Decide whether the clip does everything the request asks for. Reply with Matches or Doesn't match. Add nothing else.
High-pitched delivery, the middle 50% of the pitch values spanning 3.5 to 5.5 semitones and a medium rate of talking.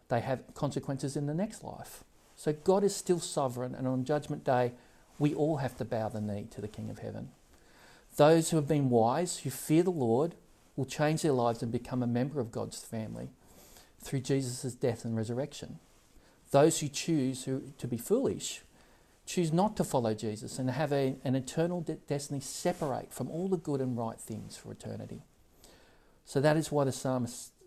Doesn't match